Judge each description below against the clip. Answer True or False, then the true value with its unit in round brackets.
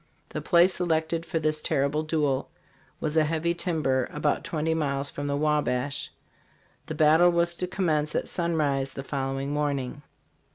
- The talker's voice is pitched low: False (155 Hz)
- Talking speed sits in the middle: True (160 wpm)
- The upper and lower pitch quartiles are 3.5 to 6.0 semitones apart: False (2.6 semitones)